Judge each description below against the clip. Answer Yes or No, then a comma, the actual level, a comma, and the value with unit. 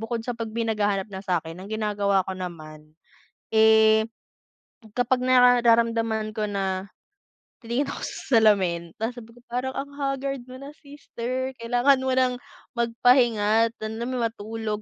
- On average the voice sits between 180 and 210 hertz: No, high, 225 Hz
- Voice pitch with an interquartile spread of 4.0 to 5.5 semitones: No, average, 3.2 semitones